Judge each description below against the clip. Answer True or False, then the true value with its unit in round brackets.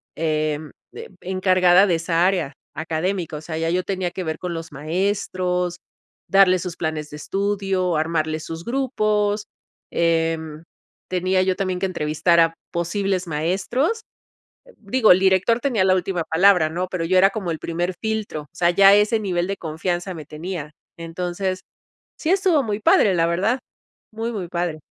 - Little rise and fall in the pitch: False (3.1 semitones)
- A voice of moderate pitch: True (180 Hz)